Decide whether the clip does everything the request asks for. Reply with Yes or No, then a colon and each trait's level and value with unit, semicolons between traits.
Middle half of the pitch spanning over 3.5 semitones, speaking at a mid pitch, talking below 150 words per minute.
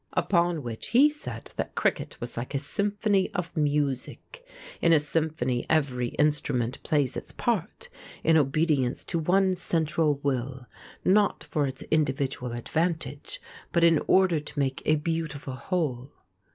Yes: average, 4.0 semitones; medium, 150 Hz; average, 140 wpm